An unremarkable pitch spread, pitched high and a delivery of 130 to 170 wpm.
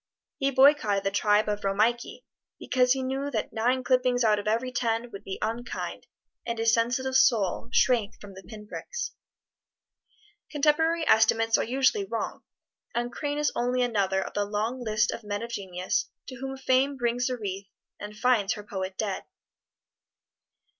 Yes: average, 3.7 semitones; high, 235 Hz; average, 165 wpm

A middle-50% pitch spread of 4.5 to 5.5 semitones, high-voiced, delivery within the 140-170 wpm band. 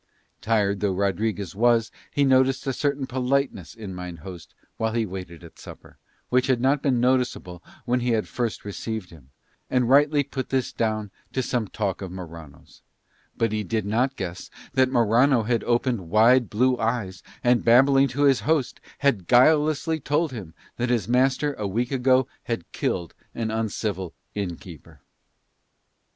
No: average, 4.8 semitones; low, 115 Hz; average, 165 wpm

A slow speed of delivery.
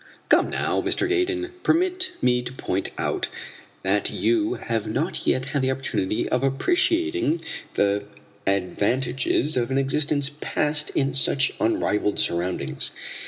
Yes: slow, 130 wpm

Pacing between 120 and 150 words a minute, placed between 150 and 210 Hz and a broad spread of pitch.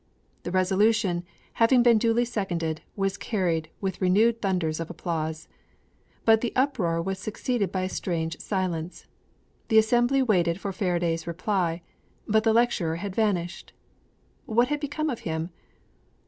No: average, 140 wpm; high, 190 Hz; average, 4.8 semitones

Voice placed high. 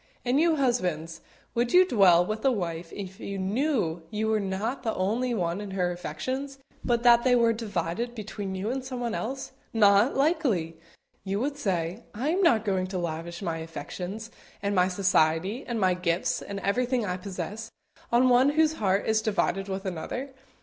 Yes: high, 205 Hz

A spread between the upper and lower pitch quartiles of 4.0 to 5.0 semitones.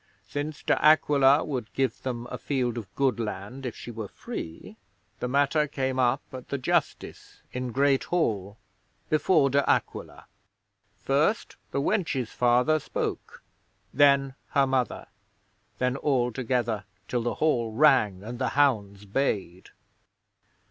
No: average, 3.5 semitones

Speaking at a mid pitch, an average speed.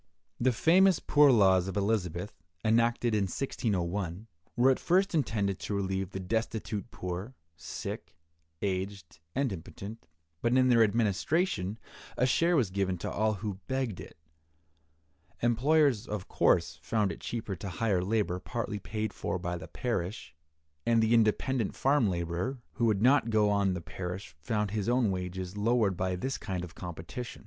No: low, 105 Hz; average, 155 wpm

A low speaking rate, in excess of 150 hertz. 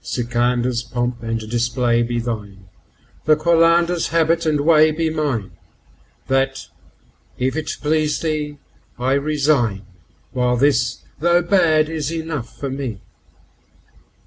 No: slow, 115 wpm; medium, 140 Hz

